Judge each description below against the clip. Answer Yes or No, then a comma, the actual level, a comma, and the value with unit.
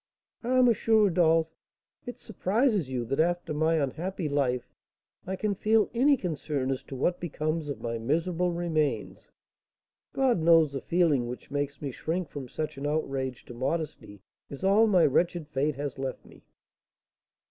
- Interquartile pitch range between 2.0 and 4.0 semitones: No, average, 4.7 semitones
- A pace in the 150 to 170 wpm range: Yes, average, 160 wpm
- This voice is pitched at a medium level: Yes, medium, 155 Hz